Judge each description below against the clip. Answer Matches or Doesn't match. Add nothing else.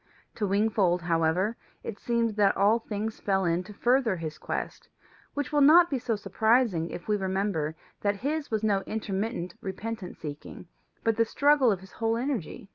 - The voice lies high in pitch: Matches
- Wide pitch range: Doesn't match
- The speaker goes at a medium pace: Matches